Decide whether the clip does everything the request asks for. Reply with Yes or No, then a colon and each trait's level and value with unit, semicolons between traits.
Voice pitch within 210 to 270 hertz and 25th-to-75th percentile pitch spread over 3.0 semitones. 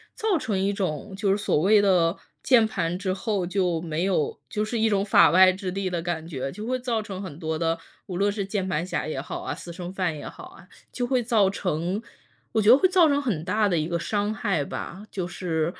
No: high, 190 Hz; average, 3.7 semitones